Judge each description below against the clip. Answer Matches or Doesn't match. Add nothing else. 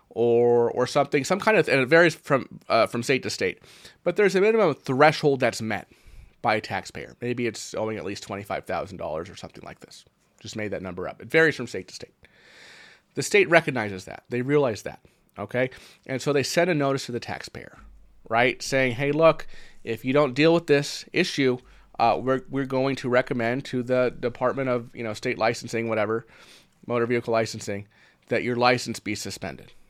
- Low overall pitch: Matches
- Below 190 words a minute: Doesn't match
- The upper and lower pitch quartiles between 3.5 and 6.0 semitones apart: Matches